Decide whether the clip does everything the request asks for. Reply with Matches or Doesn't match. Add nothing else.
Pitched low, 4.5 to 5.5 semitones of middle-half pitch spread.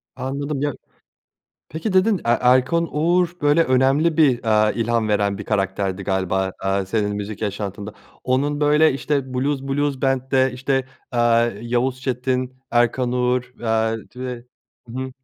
Doesn't match